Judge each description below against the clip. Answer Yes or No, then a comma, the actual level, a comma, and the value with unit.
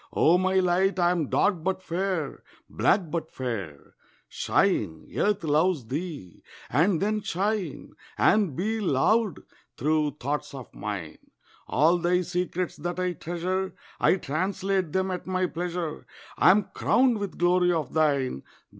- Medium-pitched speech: Yes, medium, 175 Hz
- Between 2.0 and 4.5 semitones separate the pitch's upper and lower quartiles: Yes, average, 3.8 semitones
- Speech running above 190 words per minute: No, average, 140 wpm